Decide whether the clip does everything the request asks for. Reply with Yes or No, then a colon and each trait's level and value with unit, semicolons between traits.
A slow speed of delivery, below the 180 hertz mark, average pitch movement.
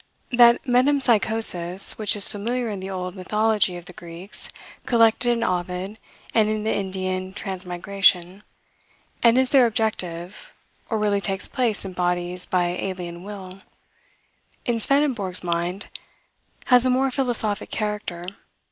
No: slow, 130 wpm; high, 200 Hz; average, 4.0 semitones